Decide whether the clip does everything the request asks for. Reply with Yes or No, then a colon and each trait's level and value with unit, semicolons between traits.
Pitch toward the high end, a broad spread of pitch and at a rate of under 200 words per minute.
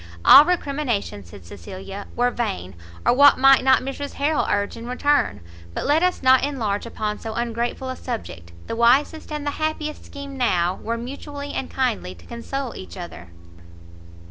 Yes: high, 245 Hz; wide, 5.8 semitones; average, 170 wpm